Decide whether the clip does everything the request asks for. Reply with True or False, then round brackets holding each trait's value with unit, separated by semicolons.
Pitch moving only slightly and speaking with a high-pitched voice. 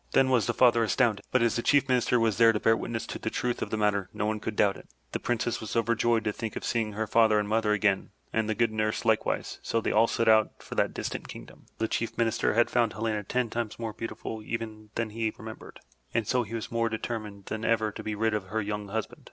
False (1.4 semitones; 110 Hz)